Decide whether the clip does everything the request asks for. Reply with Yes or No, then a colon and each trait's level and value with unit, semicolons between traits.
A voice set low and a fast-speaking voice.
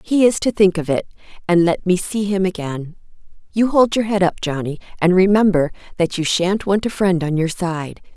No: medium, 185 Hz; fast, 215 wpm